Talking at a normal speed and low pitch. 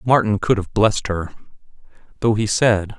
Yes: average, 160 wpm; low, 105 Hz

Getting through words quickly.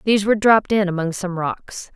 Yes: fast, 215 wpm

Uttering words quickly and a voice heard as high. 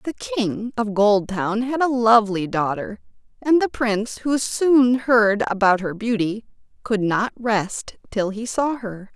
No: average, 155 wpm; high, 225 Hz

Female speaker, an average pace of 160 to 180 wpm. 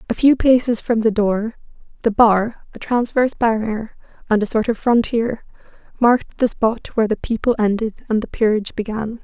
Yes: female; average, 175 wpm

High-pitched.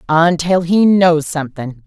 No: medium, 165 Hz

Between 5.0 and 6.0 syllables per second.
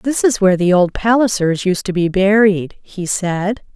No: 4.4 syllables/s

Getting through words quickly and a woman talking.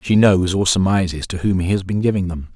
No: fast, 260 wpm; male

